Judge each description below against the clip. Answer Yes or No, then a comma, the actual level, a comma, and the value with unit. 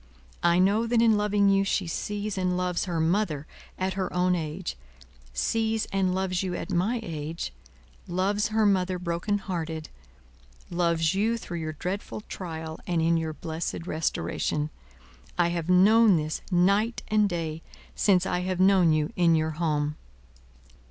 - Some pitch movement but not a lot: Yes, average, 3.4 semitones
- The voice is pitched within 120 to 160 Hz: No, medium, 180 Hz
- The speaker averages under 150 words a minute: No, average, 155 wpm